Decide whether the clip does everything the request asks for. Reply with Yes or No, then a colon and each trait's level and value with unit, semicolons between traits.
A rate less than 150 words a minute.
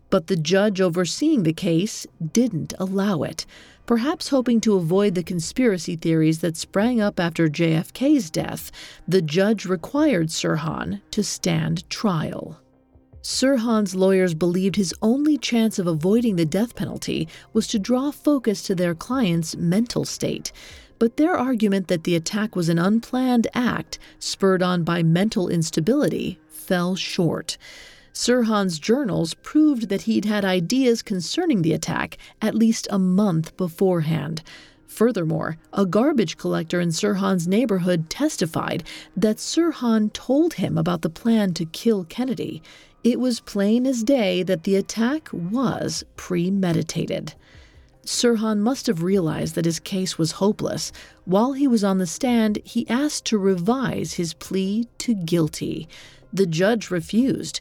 Yes: average, 140 wpm